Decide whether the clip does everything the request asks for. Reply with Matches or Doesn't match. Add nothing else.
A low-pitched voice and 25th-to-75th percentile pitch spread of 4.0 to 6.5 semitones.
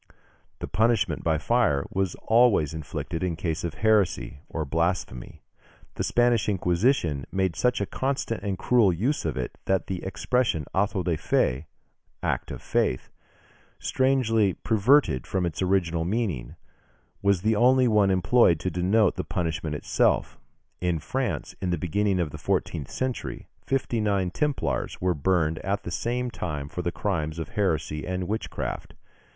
Matches